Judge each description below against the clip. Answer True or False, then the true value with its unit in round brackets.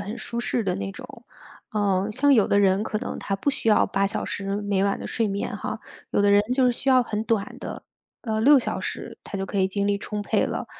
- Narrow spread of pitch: True (2.3 semitones)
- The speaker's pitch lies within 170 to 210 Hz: True (205 Hz)